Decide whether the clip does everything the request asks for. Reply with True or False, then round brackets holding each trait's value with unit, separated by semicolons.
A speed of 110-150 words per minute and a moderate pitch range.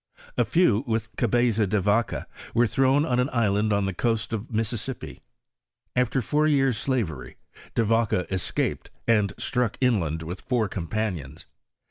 True (145 wpm; 3.7 semitones)